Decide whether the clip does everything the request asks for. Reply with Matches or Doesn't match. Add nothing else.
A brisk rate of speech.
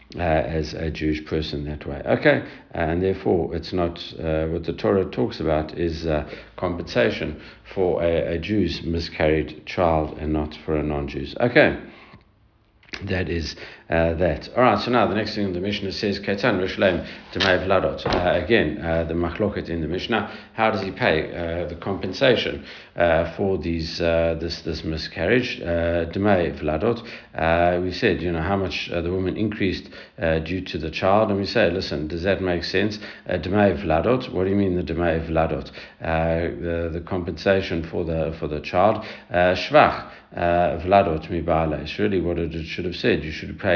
Doesn't match